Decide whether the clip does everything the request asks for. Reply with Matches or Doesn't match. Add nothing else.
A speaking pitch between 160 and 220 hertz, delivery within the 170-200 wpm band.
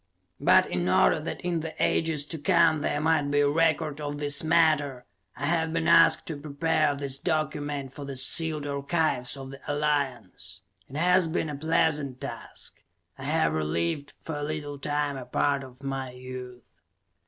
Doesn't match